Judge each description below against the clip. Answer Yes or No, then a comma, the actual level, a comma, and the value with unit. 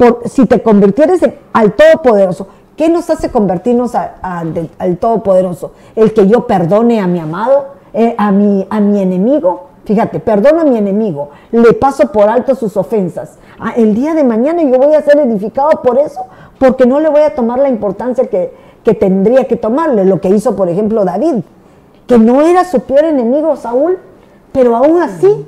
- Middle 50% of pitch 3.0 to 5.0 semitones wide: No, wide, 5.5 semitones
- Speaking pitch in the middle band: No, high, 235 Hz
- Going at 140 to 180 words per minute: No, fast, 190 wpm